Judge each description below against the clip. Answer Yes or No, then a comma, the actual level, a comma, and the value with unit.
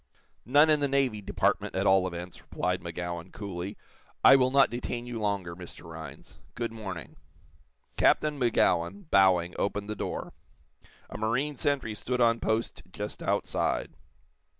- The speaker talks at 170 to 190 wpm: No, average, 145 wpm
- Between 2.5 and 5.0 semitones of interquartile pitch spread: No, wide, 5.6 semitones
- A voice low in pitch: Yes, low, 105 Hz